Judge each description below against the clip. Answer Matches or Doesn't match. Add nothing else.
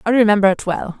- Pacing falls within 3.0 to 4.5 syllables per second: Doesn't match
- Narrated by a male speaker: Doesn't match